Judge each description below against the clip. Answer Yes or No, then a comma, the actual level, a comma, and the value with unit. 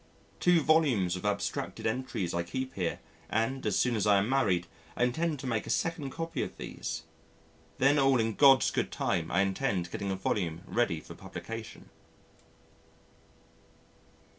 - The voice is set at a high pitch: No, low, 115 Hz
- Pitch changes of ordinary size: No, wide, 6.1 semitones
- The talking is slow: No, average, 160 wpm